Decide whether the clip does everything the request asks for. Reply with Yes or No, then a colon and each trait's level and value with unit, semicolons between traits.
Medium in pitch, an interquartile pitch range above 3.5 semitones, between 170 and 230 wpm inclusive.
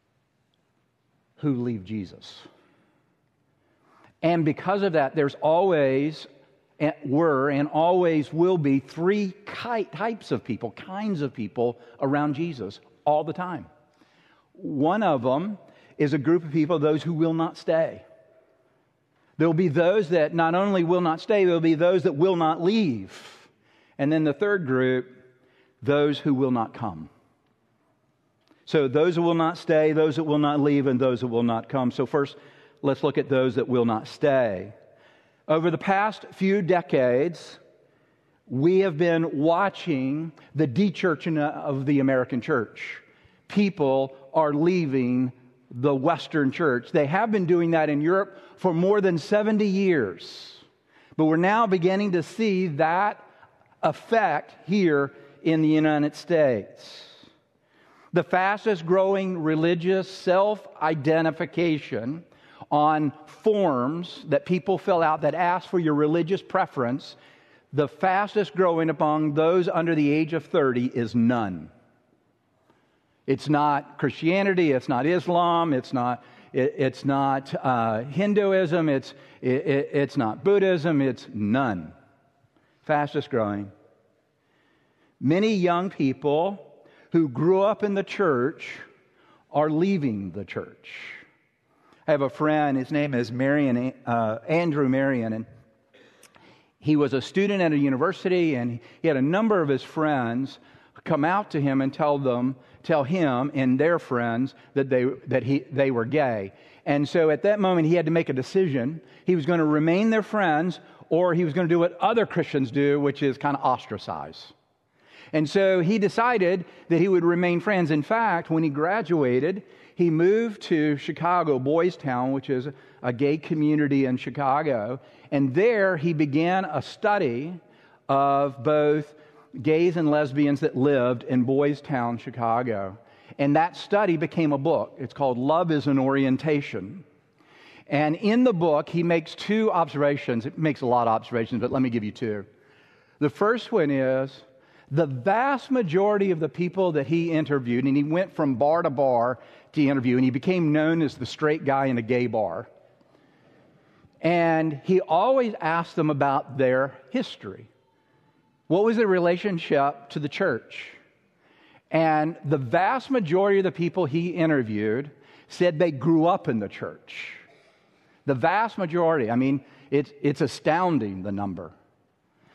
No: medium, 155 Hz; average, 4.4 semitones; average, 150 wpm